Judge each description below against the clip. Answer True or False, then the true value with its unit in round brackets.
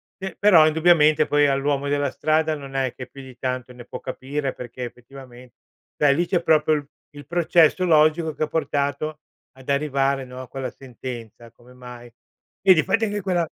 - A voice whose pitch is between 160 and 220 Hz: False (140 Hz)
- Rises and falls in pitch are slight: False (3.4 semitones)